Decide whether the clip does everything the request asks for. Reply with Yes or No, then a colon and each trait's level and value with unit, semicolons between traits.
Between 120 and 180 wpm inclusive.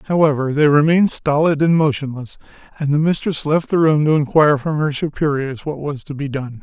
No: average, 200 wpm